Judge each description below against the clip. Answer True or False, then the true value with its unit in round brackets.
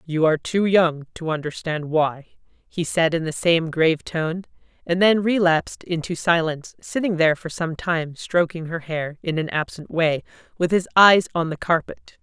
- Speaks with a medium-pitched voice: True (165 Hz)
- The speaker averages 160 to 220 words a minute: True (180 wpm)